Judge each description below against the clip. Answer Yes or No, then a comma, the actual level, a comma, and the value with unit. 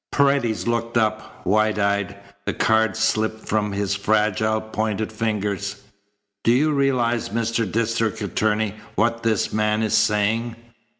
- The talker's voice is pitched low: Yes, low, 110 Hz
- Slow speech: Yes, slow, 130 wpm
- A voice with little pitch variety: Yes, narrow, 1.6 semitones